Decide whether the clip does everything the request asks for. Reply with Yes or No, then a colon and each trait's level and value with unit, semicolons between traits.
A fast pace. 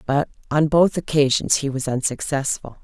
No: average, 150 wpm